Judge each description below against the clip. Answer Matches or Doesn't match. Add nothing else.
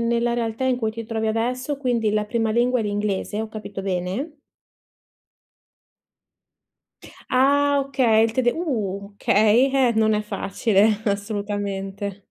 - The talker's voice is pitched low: Doesn't match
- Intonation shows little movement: Doesn't match